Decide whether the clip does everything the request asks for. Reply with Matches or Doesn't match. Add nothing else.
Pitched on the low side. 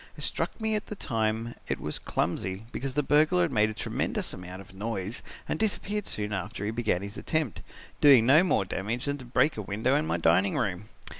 Matches